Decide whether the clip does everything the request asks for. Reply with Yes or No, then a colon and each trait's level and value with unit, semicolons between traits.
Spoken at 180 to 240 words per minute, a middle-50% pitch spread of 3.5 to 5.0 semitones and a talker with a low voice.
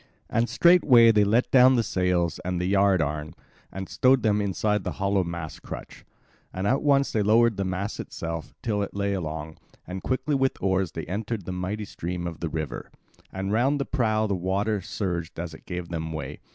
Yes: average, 200 wpm; average, 4.2 semitones; very low, 95 Hz